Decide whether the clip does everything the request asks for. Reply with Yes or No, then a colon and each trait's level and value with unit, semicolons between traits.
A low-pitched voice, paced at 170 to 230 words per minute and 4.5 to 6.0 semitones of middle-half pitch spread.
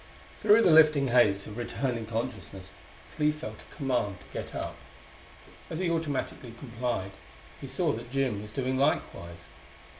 No: low, 125 Hz; average, 150 wpm; average, 5.0 semitones